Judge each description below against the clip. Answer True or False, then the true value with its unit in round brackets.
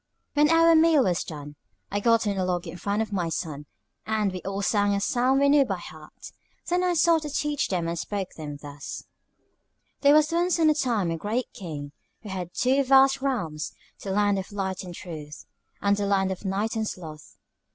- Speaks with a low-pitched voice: False (200 Hz)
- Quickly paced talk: True (215 wpm)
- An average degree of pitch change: False (7.4 semitones)